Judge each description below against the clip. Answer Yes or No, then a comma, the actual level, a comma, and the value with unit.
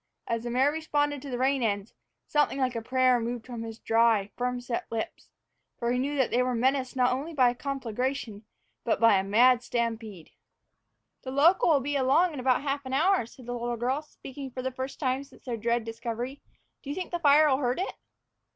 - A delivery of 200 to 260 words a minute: Yes, fast, 205 wpm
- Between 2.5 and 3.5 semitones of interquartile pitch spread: Yes, average, 2.9 semitones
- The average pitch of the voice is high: Yes, very high, 255 Hz